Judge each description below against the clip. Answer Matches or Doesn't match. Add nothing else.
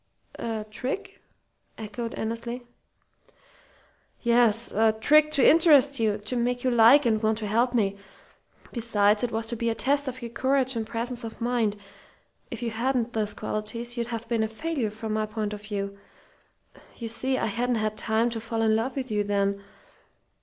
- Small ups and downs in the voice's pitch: Matches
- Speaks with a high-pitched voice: Matches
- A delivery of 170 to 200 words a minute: Matches